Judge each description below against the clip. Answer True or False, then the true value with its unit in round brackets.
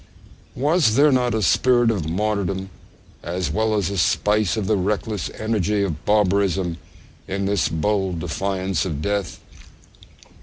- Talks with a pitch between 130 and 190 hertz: False (100 Hz)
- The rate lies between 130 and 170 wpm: True (140 wpm)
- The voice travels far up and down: False (2.8 semitones)